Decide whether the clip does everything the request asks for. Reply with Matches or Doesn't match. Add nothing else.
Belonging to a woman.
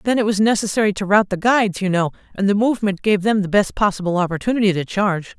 Matches